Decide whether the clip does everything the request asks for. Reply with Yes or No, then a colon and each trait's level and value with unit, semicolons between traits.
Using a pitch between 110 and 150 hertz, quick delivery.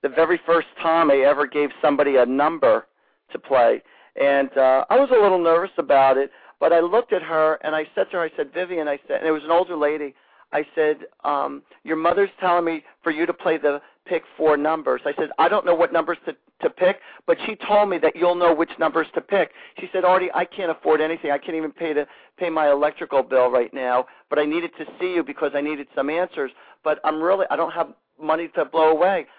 No: medium, 160 Hz; fast, 240 wpm